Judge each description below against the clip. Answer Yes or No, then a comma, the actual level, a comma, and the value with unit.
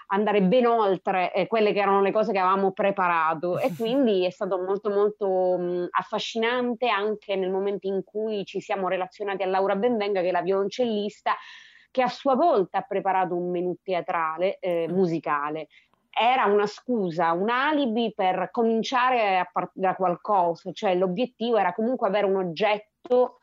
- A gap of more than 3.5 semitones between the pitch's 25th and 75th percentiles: No, average, 3.2 semitones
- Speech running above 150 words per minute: Yes, average, 165 wpm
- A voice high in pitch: Yes, high, 195 Hz